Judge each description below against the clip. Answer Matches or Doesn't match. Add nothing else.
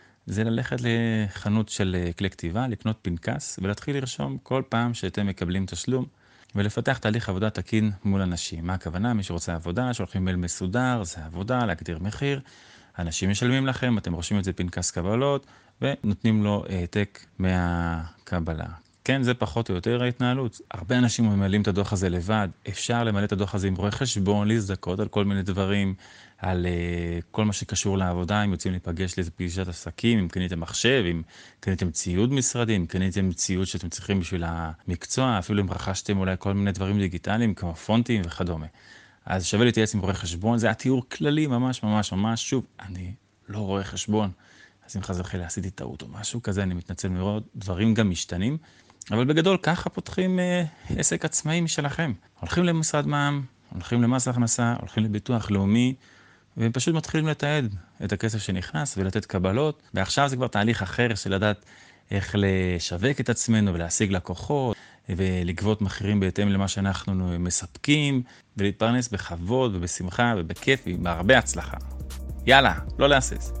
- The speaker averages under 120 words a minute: Doesn't match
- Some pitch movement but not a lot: Matches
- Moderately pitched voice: Doesn't match